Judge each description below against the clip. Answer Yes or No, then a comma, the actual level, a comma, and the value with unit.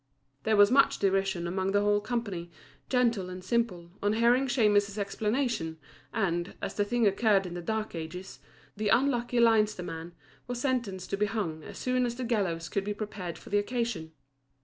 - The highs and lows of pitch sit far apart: No, average, 4.2 semitones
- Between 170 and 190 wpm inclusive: Yes, average, 180 wpm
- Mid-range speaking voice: No, high, 205 Hz